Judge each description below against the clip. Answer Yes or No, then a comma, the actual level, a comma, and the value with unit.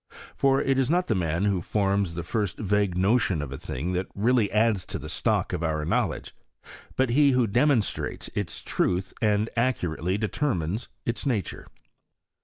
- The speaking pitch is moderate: No, low, 105 Hz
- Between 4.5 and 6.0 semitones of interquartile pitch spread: Yes, average, 5.0 semitones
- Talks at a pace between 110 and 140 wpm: No, average, 175 wpm